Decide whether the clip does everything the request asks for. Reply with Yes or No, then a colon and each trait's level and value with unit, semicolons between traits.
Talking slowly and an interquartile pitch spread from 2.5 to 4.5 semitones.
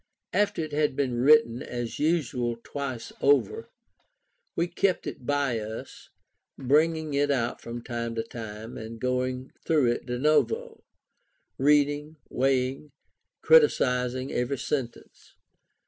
Yes: slow, 125 wpm; average, 3.8 semitones